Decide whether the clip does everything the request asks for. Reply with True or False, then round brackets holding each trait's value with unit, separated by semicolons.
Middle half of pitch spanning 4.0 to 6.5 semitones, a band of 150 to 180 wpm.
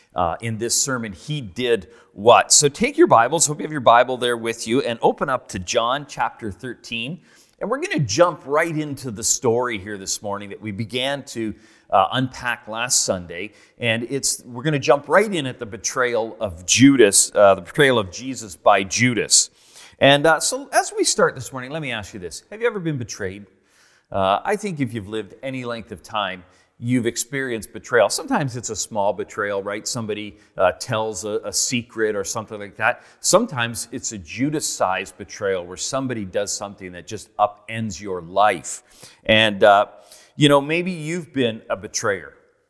False (5.1 semitones; 195 wpm)